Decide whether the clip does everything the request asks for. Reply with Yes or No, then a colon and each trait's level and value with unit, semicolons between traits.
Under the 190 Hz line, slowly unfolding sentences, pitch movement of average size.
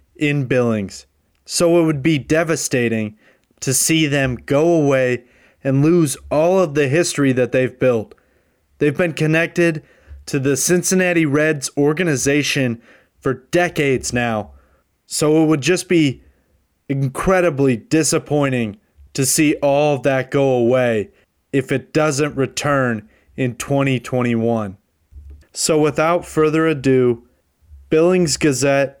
Yes: medium, 140 Hz; slow, 120 wpm; average, 4.5 semitones